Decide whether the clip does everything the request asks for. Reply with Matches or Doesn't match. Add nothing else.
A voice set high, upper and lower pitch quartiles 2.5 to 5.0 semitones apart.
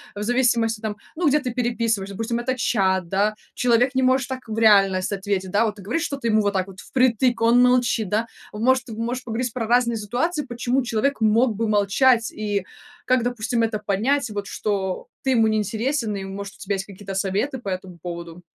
Matches